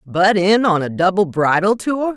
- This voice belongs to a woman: Yes, female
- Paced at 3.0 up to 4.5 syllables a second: Yes, 4.4 syllables/s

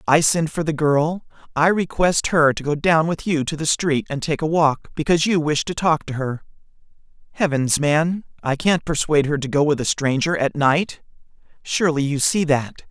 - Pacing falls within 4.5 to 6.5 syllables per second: Yes, 5.0 syllables/s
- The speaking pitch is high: No, medium, 155 Hz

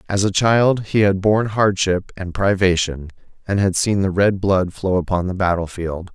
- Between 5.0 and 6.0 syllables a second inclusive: No, 4.7 syllables/s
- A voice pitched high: No, very low, 95 Hz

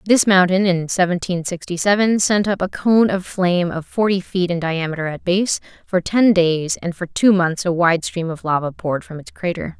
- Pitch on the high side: No, medium, 180 Hz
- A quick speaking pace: Yes, fast, 215 wpm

